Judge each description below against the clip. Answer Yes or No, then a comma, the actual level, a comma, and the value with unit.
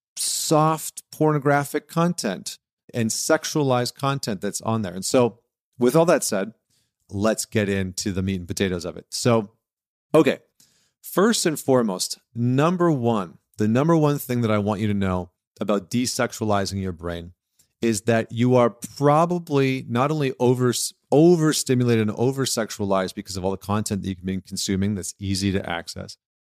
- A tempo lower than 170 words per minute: Yes, average, 155 wpm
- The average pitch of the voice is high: No, low, 115 Hz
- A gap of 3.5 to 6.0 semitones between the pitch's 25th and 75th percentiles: Yes, wide, 5.6 semitones